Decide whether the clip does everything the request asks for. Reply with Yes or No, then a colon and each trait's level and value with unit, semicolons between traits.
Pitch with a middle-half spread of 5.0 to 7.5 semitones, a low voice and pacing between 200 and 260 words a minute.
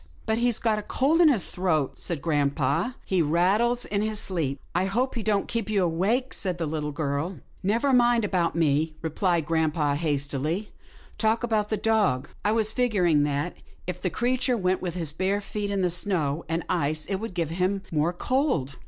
No: wide, 5.5 semitones; medium, 185 Hz; fast, 205 wpm